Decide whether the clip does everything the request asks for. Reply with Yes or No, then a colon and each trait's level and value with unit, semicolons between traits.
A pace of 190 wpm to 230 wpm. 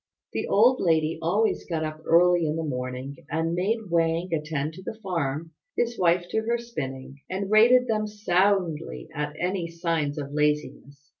No: average, 165 wpm